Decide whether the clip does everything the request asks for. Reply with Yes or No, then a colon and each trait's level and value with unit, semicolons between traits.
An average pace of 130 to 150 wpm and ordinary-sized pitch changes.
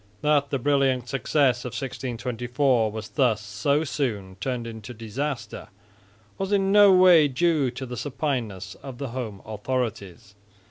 Yes: average, 140 wpm; average, 4.2 semitones